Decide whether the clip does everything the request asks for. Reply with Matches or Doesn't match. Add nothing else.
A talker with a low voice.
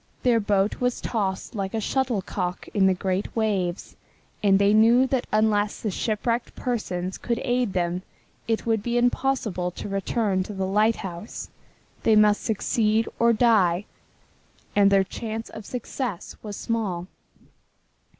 Doesn't match